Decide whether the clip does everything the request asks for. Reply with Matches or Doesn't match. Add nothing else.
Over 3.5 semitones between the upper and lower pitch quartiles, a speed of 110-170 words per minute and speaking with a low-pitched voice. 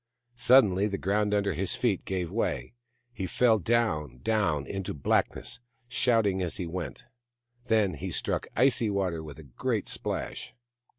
Matches